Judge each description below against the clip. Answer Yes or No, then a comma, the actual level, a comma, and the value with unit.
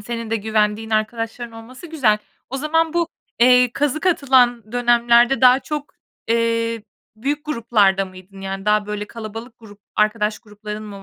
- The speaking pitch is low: No, high, 230 Hz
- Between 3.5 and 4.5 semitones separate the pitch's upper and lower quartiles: No, average, 3.0 semitones